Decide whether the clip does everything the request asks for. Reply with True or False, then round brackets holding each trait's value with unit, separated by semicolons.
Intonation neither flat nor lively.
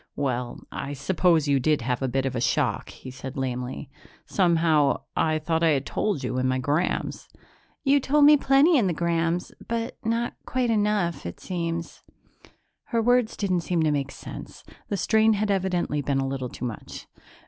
False (7.5 semitones)